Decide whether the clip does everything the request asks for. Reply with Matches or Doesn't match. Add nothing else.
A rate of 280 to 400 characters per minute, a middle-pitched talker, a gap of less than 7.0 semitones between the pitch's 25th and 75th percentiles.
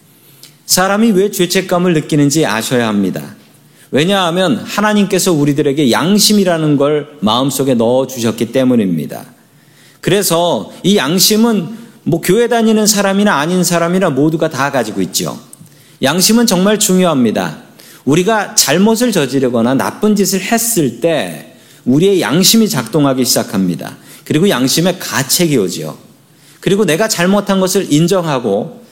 Matches